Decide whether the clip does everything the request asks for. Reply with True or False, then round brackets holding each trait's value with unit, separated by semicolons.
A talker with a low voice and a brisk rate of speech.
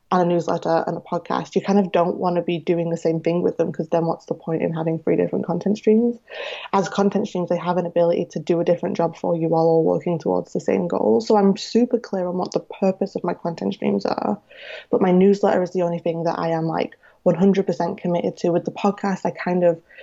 False (175 Hz; 250 wpm)